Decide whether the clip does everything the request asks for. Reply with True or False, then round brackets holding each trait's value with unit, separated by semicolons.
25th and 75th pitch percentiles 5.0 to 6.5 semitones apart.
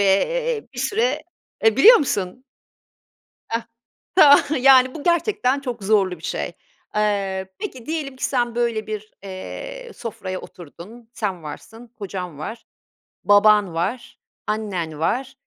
True (5.6 semitones)